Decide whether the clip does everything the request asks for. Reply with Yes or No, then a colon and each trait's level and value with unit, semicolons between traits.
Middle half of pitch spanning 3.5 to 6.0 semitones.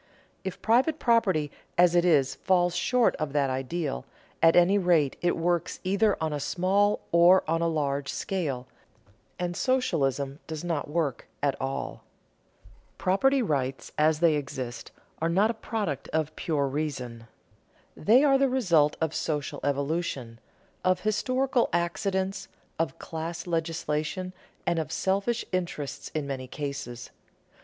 Yes: average, 4.8 semitones